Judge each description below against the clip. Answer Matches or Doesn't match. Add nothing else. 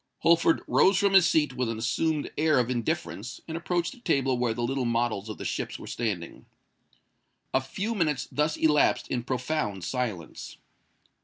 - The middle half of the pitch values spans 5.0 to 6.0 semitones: Matches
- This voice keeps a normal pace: Matches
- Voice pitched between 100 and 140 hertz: Matches